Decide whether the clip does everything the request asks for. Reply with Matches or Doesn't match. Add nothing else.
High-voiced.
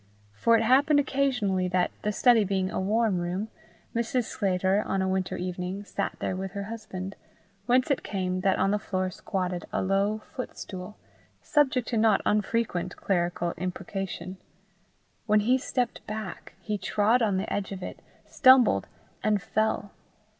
Matches